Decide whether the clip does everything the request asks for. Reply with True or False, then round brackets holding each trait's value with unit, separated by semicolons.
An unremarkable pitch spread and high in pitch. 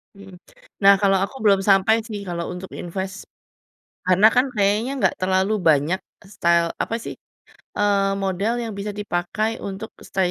False (1.9 semitones; 195 Hz)